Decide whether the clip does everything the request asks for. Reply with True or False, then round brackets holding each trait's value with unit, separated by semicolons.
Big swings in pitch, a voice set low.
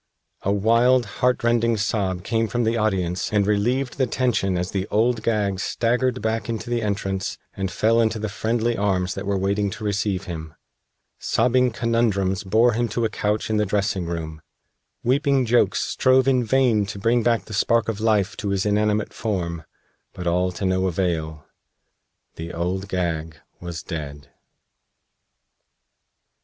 False (3.7 semitones; 105 Hz)